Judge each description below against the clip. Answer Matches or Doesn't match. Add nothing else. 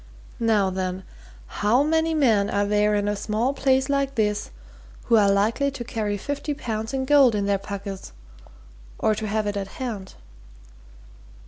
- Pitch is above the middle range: Matches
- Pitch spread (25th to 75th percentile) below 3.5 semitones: Doesn't match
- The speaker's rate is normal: Matches